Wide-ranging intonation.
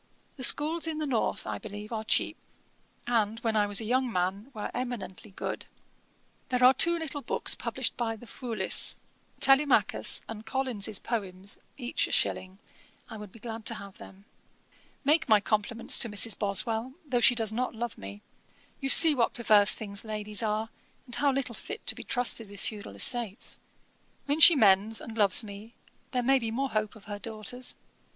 No: average, 3.5 semitones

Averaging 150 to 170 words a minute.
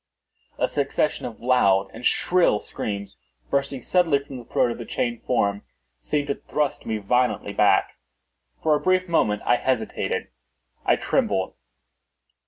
No: average, 140 wpm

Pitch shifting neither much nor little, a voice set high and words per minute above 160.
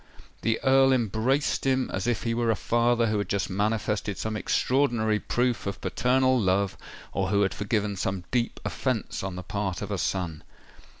No: average, 3.5 semitones; low, 110 Hz; average, 185 wpm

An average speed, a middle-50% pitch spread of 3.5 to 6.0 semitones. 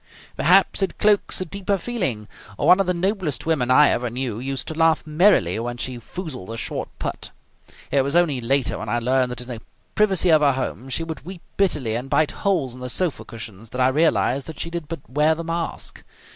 No: fast, 215 wpm; wide, 5.5 semitones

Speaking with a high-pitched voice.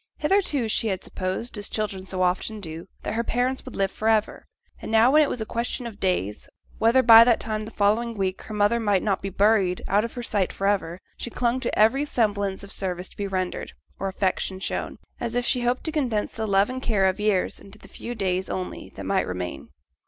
Yes: high, 210 Hz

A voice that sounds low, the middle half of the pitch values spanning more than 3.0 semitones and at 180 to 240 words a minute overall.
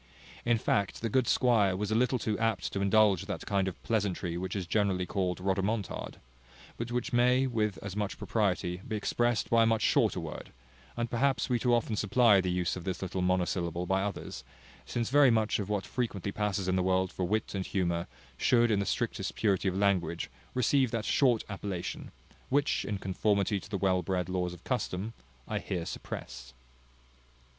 Yes: low, 100 Hz; average, 3.5 semitones; average, 190 wpm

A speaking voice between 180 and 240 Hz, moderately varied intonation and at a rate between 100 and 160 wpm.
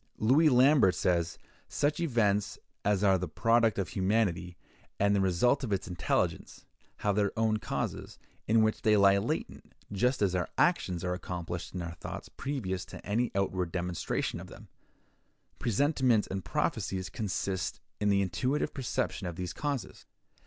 No: low, 100 Hz; average, 4.3 semitones; average, 155 wpm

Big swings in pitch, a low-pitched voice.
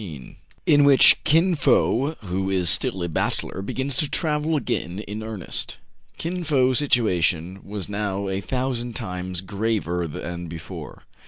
Yes: wide, 6.7 semitones; low, 105 Hz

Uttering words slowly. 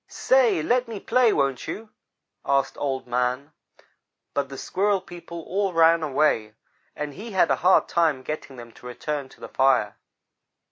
No: average, 160 wpm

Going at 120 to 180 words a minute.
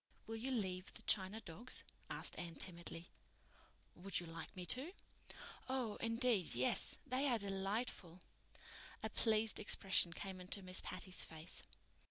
Yes: average, 140 wpm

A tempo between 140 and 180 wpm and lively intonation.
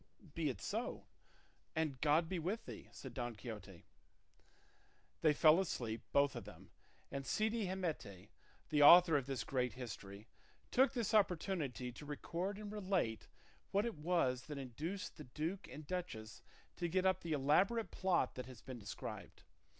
Yes: average, 160 wpm; wide, 6.7 semitones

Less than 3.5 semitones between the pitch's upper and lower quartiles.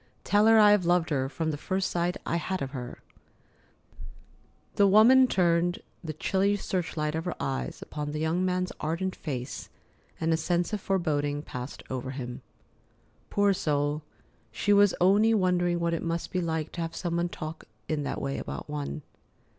No: average, 3.8 semitones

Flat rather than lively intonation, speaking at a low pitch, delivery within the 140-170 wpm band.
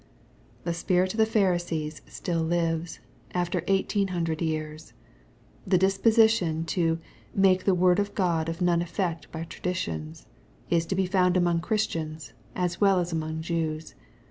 No: narrow, 2.3 semitones; medium, 175 Hz; average, 150 wpm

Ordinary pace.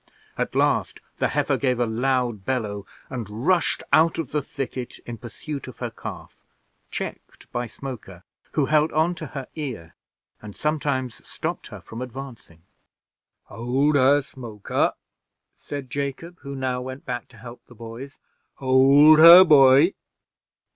Yes: average, 145 wpm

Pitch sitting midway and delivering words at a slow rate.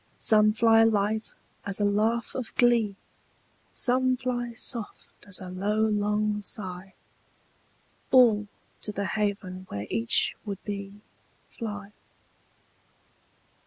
No: high, 210 Hz; slow, 110 wpm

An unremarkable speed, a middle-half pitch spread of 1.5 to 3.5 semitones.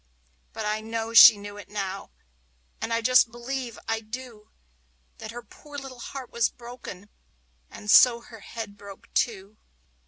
Yes: average, 160 wpm; narrow, 2.5 semitones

